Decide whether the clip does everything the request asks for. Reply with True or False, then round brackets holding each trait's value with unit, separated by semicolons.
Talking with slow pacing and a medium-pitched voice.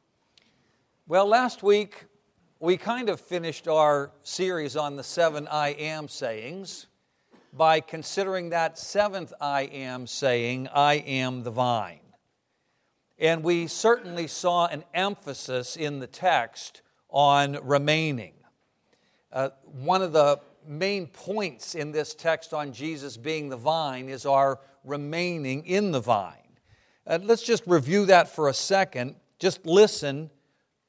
True (130 wpm; 155 Hz)